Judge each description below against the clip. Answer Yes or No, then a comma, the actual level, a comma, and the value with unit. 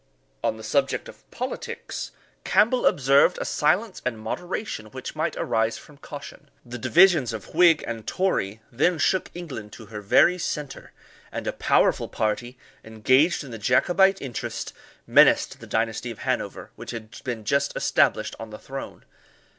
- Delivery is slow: No, average, 155 wpm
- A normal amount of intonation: No, wide, 6.5 semitones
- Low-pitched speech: Yes, low, 130 Hz